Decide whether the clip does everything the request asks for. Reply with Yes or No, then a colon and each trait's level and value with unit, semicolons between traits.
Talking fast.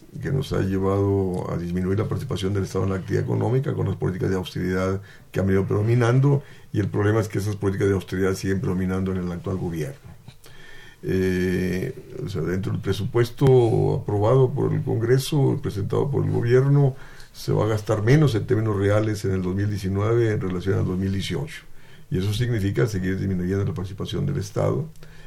No: average, 180 wpm